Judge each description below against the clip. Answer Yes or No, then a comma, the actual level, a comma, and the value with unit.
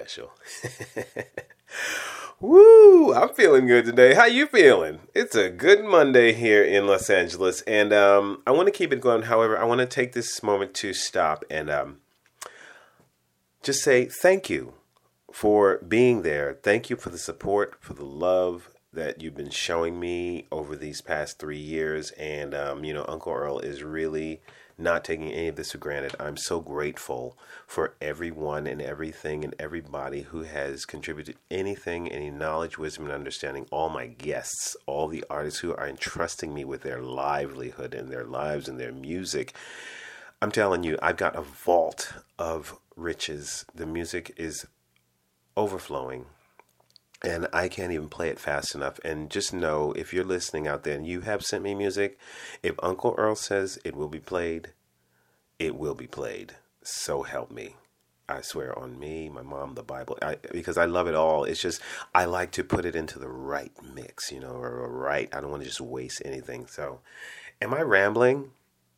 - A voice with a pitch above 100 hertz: No, very low, 85 Hz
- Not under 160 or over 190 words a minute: Yes, average, 175 wpm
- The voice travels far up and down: Yes, wide, 6.6 semitones